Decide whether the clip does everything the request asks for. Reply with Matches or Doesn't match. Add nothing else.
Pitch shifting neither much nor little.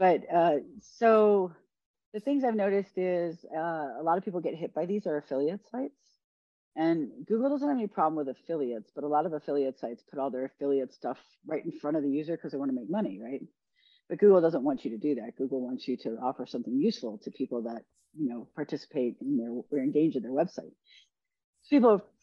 Doesn't match